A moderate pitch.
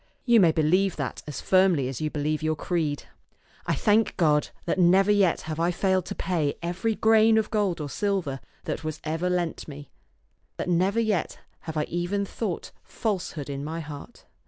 Yes: medium, 175 Hz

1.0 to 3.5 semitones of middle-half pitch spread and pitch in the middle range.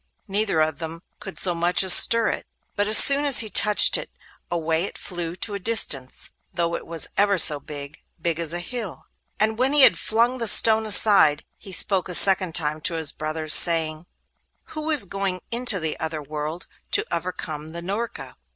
No: average, 5.0 semitones; medium, 180 Hz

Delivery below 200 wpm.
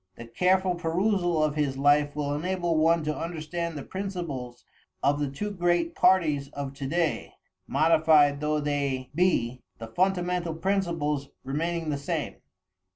Yes: average, 145 wpm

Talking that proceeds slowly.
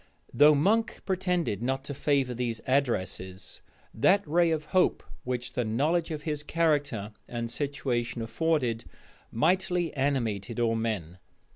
Yes: slow, 130 wpm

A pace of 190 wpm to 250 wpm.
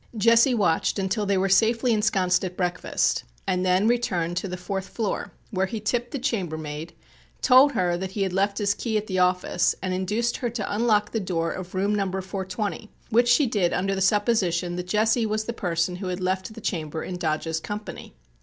Yes: average, 200 wpm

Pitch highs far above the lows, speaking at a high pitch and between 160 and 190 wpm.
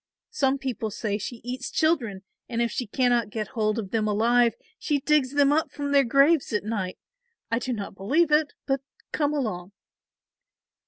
No: average, 4.9 semitones; high, 245 Hz; average, 175 wpm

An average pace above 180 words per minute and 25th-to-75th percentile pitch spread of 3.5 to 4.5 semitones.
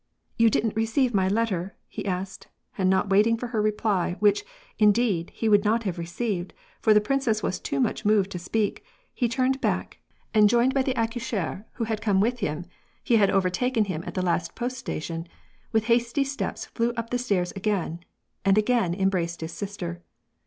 Yes: average, 190 wpm; average, 3.8 semitones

